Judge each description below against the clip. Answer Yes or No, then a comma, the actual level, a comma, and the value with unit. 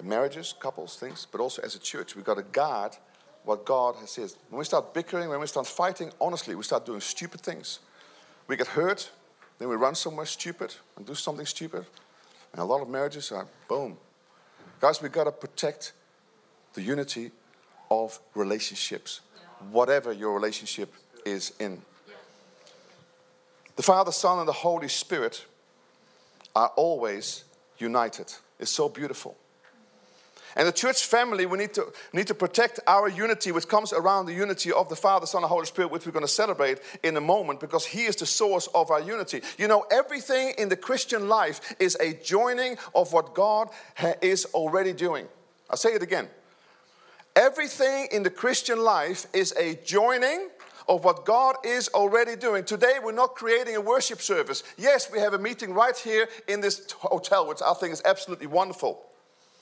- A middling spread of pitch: No, wide, 6.5 semitones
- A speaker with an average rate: Yes, average, 175 wpm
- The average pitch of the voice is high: Yes, high, 195 Hz